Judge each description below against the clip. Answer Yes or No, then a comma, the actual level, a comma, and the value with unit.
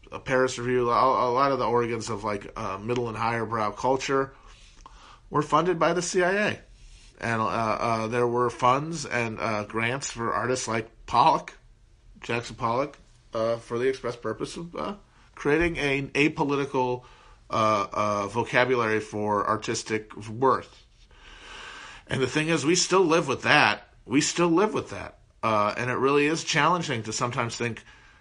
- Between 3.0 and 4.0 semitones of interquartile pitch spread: Yes, average, 3.5 semitones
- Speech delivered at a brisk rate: No, average, 160 wpm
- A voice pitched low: Yes, low, 120 Hz